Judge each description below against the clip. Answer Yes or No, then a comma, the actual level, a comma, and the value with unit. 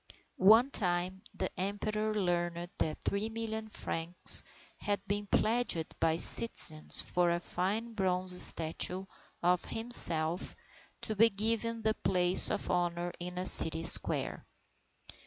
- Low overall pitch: No, medium, 185 Hz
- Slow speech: Yes, slow, 120 wpm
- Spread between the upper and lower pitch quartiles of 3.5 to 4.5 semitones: Yes, average, 3.8 semitones